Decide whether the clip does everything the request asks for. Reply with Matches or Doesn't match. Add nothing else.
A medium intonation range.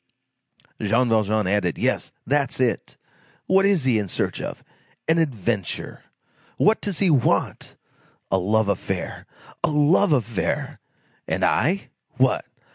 Doesn't match